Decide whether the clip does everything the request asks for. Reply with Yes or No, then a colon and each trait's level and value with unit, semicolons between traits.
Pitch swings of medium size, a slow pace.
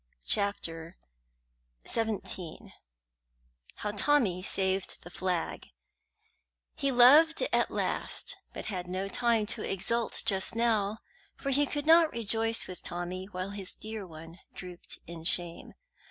Yes: average, 4.3 semitones; slow, 125 wpm